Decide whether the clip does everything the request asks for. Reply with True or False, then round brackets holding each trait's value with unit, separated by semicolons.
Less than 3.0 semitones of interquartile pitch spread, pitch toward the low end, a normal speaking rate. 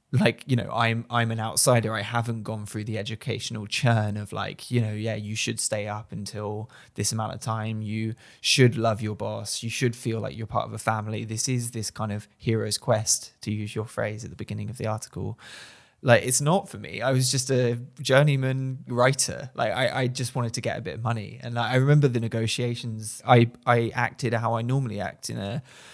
False (2.5 semitones; 115 Hz; 225 wpm)